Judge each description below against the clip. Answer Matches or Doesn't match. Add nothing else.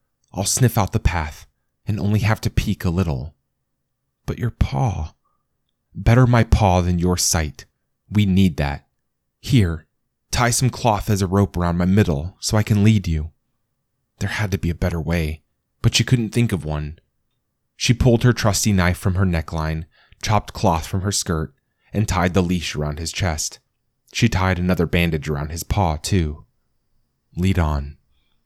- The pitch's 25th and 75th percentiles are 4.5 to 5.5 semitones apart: Matches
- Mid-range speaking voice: Doesn't match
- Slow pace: Doesn't match